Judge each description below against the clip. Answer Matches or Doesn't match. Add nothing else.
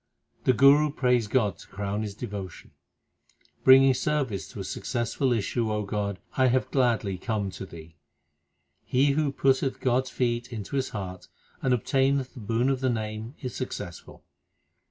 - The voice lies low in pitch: Matches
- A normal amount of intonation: Matches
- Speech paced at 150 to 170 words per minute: Matches